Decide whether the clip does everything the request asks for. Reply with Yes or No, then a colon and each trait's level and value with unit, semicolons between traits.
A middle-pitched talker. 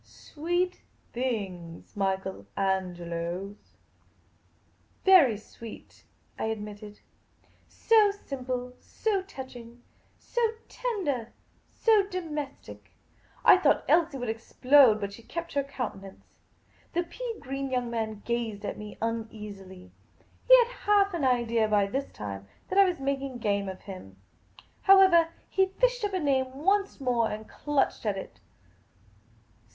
No: very high, 250 Hz